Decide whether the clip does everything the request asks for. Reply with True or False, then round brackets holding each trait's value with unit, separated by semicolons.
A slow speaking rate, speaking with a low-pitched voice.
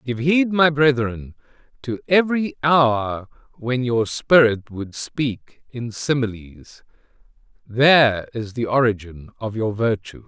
True (125 wpm; 125 Hz)